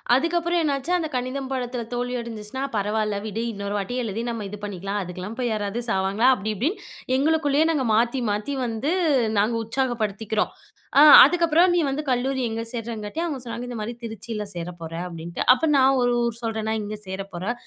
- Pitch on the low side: No, high, 230 Hz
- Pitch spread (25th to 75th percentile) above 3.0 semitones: Yes, average, 4.2 semitones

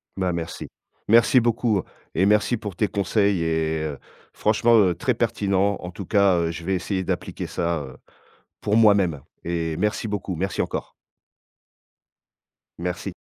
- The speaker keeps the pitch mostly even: No, average, 3.6 semitones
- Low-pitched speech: Yes, very low, 95 Hz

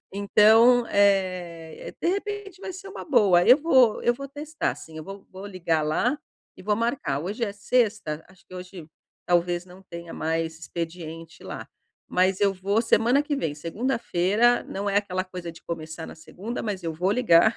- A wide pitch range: Yes, wide, 5.7 semitones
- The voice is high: Yes, high, 195 Hz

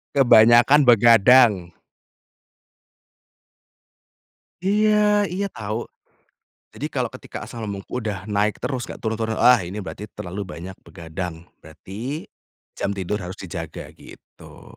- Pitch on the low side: Yes, low, 105 Hz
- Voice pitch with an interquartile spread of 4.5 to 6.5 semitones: Yes, average, 4.9 semitones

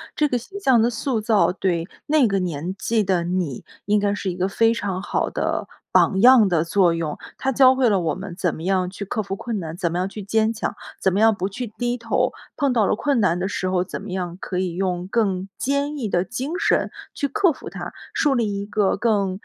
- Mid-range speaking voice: No, high, 200 Hz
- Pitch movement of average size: Yes, average, 4.3 semitones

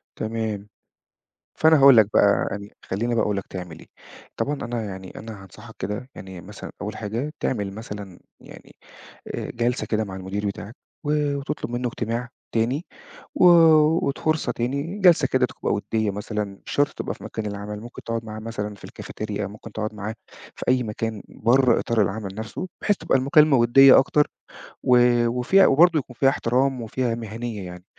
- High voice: No, low, 115 Hz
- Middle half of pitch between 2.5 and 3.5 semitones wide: No, average, 4.0 semitones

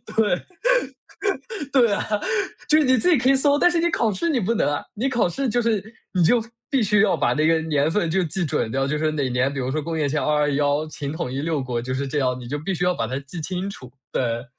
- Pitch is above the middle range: No, medium, 160 Hz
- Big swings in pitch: Yes, wide, 7.9 semitones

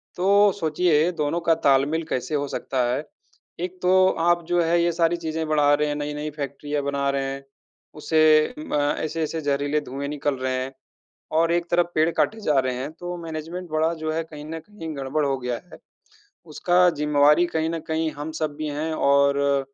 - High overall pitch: No, medium, 155 Hz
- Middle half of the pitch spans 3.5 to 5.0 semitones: No, narrow, 2.6 semitones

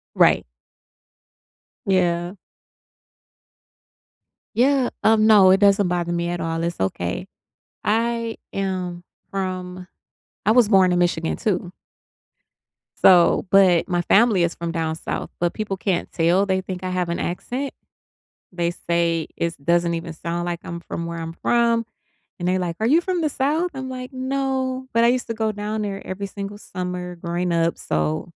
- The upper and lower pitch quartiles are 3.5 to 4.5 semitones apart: Yes, average, 4.2 semitones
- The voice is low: No, medium, 185 Hz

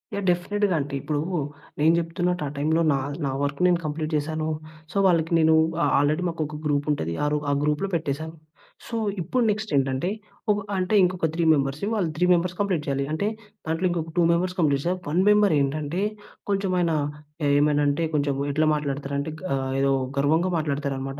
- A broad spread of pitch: No, average, 3.7 semitones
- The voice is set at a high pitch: No, medium, 155 Hz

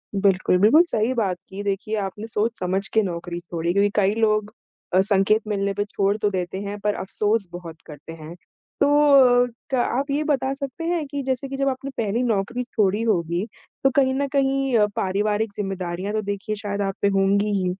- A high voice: Yes, high, 205 Hz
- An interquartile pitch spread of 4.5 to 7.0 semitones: No, average, 3.9 semitones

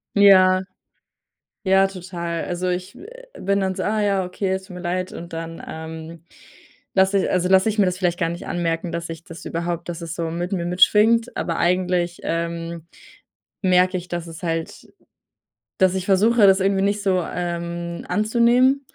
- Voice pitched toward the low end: No, medium, 180 Hz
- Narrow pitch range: Yes, narrow, 2.2 semitones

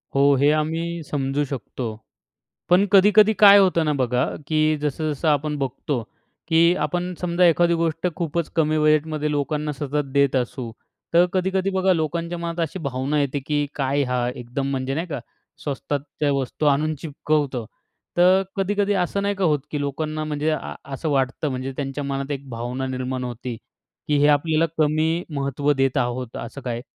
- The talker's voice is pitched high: No, medium, 150 Hz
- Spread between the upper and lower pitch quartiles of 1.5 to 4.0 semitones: Yes, average, 3.5 semitones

